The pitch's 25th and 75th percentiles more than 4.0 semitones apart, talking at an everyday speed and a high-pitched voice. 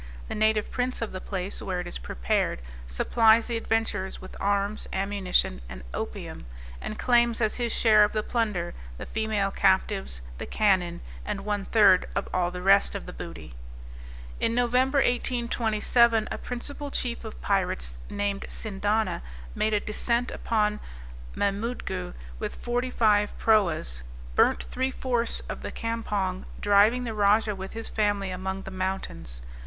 No: average, 3.3 semitones; average, 150 wpm; high, 210 Hz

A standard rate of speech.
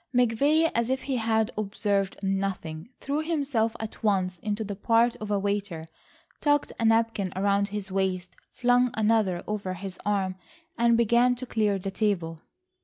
Yes: average, 160 wpm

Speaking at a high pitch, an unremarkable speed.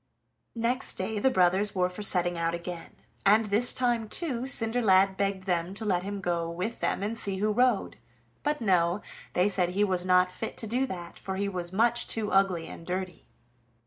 Yes: high, 195 Hz; average, 195 wpm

